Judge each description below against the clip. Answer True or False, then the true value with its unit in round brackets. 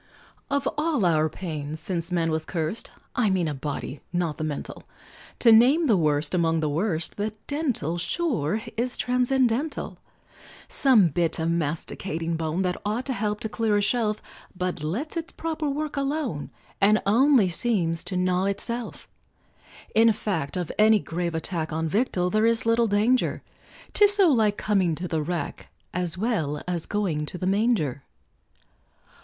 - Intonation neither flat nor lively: False (6.2 semitones)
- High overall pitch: True (195 Hz)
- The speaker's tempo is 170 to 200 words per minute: False (160 wpm)